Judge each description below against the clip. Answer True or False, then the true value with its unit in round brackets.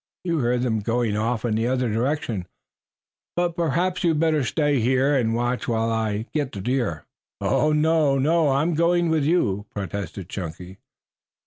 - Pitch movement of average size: False (5.7 semitones)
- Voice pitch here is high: False (125 Hz)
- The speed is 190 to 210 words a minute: False (160 wpm)